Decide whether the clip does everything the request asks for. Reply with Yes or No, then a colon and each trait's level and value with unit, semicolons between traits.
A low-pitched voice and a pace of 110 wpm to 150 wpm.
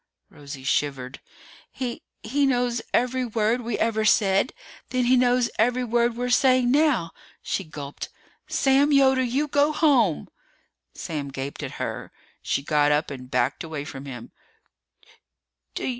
No: high, 235 Hz; average, 140 wpm